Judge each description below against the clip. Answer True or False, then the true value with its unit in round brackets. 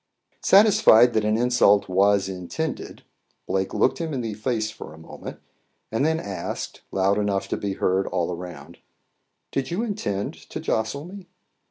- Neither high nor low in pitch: False (110 Hz)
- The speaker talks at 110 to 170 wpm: True (160 wpm)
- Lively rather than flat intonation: True (6.0 semitones)